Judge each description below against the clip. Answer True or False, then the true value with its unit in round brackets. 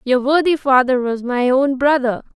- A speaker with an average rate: True (175 wpm)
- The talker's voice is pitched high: True (260 Hz)